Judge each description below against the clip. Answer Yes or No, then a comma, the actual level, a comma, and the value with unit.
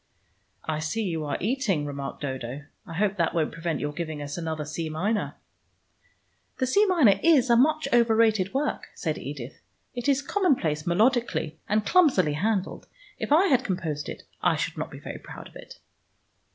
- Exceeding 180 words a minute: No, average, 175 wpm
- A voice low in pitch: No, high, 195 Hz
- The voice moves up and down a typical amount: No, wide, 8.4 semitones